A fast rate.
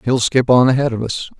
Yes: fast, 260 wpm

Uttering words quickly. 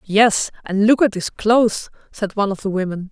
Yes: fast, 210 wpm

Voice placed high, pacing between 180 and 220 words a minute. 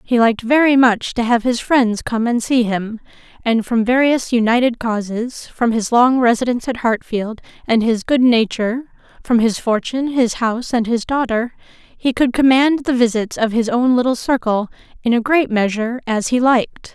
Yes: high, 240 Hz; average, 185 wpm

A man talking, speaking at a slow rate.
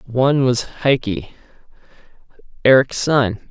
Yes: male; slow, 85 wpm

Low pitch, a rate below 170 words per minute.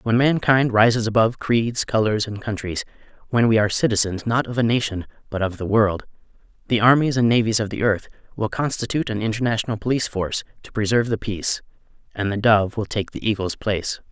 No: low, 110 Hz; average, 190 wpm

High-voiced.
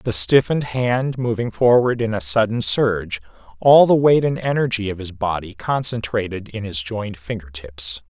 No: low, 110 Hz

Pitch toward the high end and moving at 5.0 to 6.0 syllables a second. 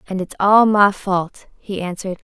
No: high, 195 Hz; 4.6 syllables/s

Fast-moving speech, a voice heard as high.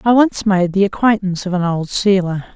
Yes: fast, 210 wpm; high, 195 Hz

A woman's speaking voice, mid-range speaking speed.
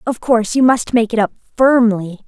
No: female; fast, 210 wpm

